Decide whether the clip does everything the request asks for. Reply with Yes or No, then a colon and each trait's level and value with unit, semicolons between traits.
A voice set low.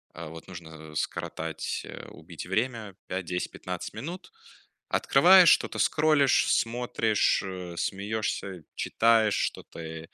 Yes: low, 100 Hz